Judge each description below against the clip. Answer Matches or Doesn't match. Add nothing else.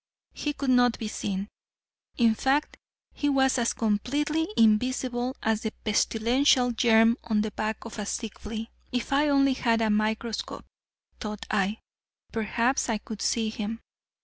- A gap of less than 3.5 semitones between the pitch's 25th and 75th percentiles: Matches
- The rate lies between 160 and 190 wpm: Doesn't match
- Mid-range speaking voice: Doesn't match